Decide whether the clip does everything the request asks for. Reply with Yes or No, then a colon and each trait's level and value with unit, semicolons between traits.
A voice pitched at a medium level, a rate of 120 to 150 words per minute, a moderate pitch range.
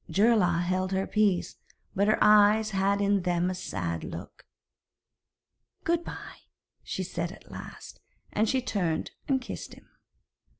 No: high, 195 Hz; average, 140 wpm; average, 3.1 semitones